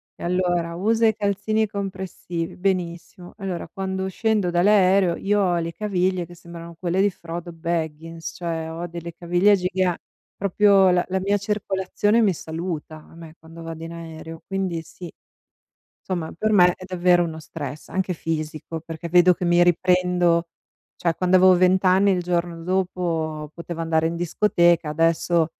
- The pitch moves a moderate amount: No, narrow, 2.3 semitones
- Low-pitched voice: No, medium, 175 Hz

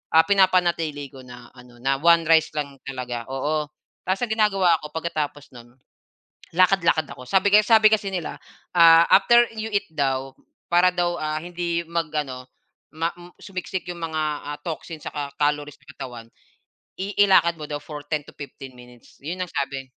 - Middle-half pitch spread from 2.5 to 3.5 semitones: No, average, 4.2 semitones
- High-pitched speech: No, medium, 160 Hz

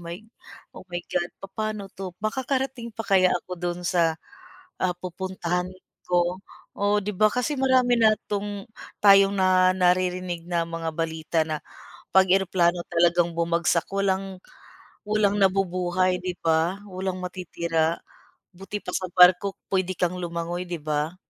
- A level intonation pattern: Yes, narrow, 2.2 semitones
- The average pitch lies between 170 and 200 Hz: Yes, medium, 185 Hz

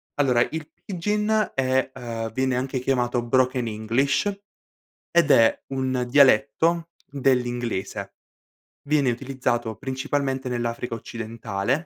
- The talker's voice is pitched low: Yes, low, 130 Hz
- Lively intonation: No, narrow, 2.6 semitones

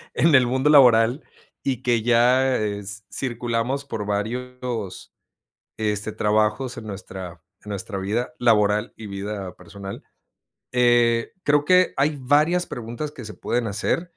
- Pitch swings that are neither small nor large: Yes, average, 3.7 semitones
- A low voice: Yes, low, 115 Hz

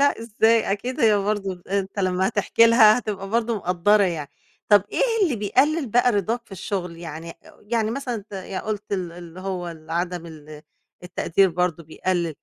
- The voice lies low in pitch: No, high, 195 Hz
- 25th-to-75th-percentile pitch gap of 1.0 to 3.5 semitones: No, average, 3.9 semitones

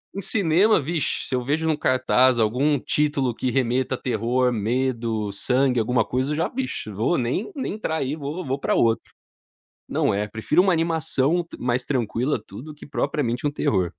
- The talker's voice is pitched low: Yes, low, 130 Hz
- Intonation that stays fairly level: No, average, 4.3 semitones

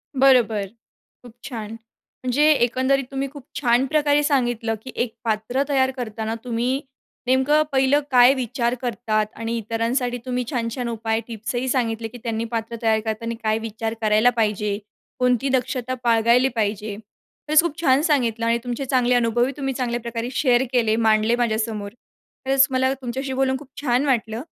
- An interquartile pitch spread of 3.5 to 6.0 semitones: No, average, 2.7 semitones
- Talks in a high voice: Yes, high, 240 Hz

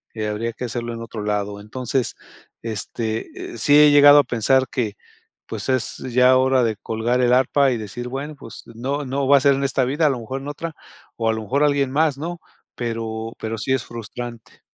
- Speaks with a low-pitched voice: Yes, low, 125 Hz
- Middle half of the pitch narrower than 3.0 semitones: No, average, 3.4 semitones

